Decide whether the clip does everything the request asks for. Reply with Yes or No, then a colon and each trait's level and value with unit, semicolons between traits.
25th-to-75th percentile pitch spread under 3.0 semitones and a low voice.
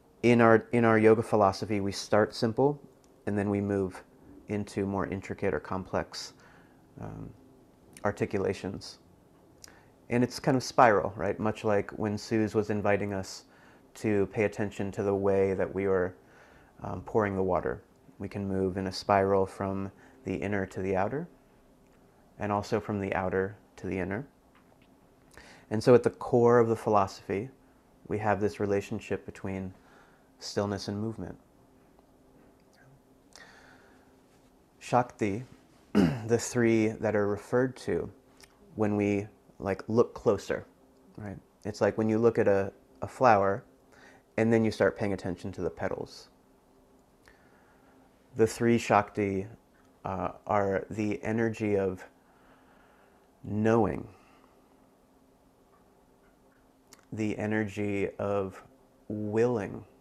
Yes: narrow, 2.5 semitones; low, 100 Hz